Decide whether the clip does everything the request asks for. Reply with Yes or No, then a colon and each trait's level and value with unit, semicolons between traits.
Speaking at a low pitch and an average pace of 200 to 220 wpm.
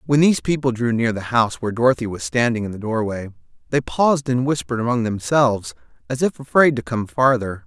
Yes: low, 120 Hz; fast, 205 wpm